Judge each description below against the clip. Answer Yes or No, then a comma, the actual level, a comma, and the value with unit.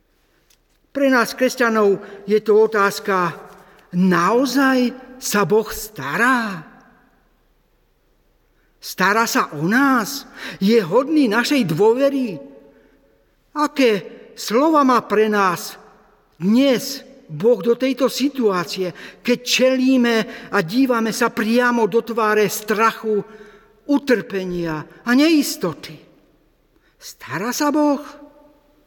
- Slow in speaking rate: Yes, slow, 90 wpm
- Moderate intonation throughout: Yes, average, 4.2 semitones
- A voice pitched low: No, high, 235 Hz